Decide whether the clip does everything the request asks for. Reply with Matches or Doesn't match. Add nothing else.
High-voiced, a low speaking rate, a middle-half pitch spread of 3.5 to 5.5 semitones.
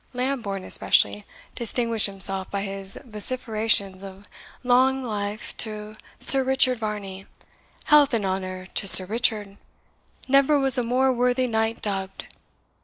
Matches